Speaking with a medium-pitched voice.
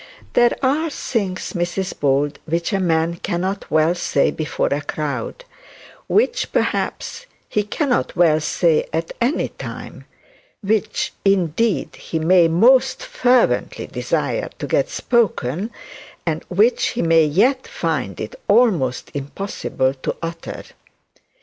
Yes: medium, 175 Hz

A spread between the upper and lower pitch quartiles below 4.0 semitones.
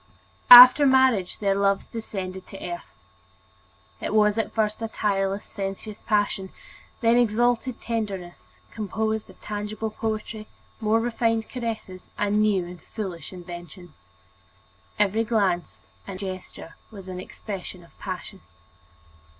Yes: average, 3.0 semitones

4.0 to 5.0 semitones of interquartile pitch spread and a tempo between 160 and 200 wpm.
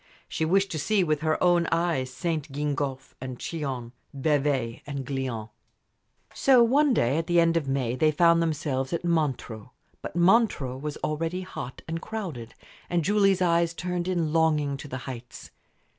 Yes: average, 4.4 semitones; average, 165 wpm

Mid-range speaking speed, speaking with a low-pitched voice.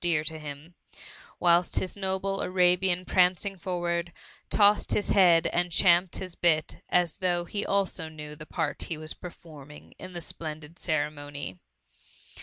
No: average, 150 wpm; medium, 175 Hz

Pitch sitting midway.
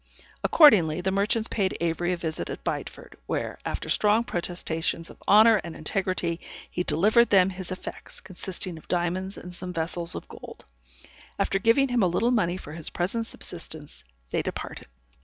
Yes: medium, 180 Hz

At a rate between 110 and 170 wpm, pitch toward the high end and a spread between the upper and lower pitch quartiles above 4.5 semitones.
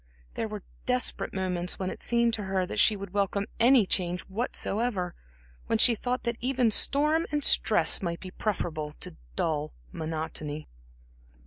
Yes: average, 155 wpm; high, 200 Hz; average, 5.0 semitones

